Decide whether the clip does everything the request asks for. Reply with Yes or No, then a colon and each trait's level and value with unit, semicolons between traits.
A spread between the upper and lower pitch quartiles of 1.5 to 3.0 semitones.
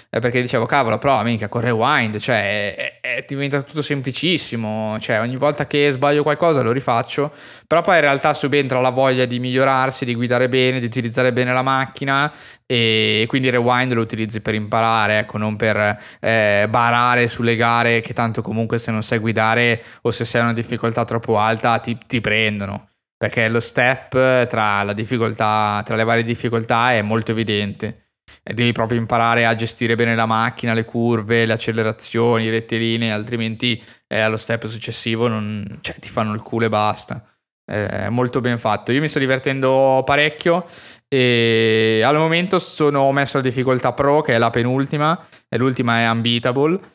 Yes: narrow, 2.5 semitones